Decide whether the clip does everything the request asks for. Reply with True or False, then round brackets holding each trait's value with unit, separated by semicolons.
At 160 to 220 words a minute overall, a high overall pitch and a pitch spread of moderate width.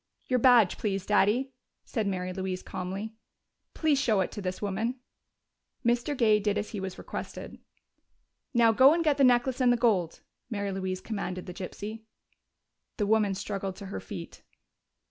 True (165 wpm; 210 Hz; 4.0 semitones)